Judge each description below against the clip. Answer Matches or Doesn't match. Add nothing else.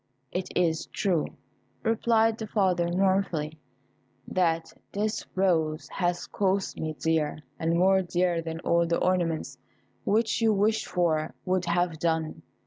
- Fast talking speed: Doesn't match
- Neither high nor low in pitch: Matches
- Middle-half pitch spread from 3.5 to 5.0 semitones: Doesn't match